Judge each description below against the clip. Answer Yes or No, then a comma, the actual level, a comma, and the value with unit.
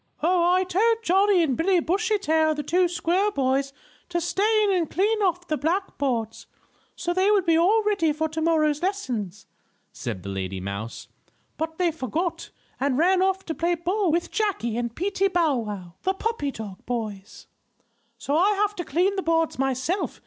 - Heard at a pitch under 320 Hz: No, very high, 335 Hz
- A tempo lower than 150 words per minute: No, average, 180 wpm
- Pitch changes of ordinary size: No, wide, 5.8 semitones